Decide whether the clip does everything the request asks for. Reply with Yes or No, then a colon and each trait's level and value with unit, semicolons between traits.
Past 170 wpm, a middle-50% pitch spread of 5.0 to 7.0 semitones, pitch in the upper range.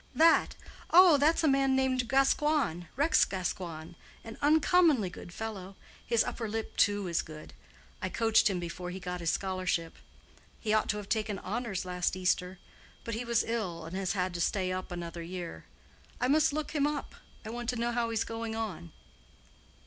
Yes: average, 180 wpm; wide, 5.6 semitones; high, 215 Hz